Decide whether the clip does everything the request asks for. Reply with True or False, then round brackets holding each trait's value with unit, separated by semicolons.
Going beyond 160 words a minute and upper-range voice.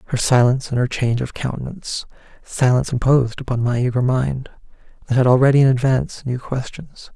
False (170 wpm; 125 Hz)